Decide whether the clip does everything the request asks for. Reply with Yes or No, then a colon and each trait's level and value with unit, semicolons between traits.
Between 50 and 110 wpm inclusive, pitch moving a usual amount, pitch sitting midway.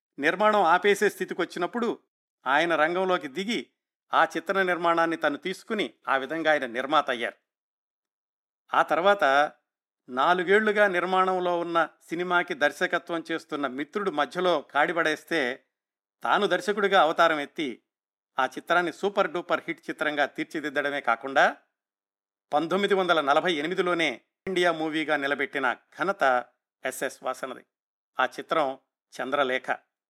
Yes: average, 105 wpm; average, 4.2 semitones; medium, 165 Hz